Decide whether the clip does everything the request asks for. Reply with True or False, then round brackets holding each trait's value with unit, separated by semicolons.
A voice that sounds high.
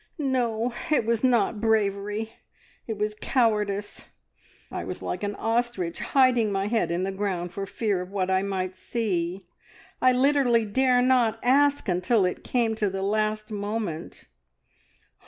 True (215 Hz)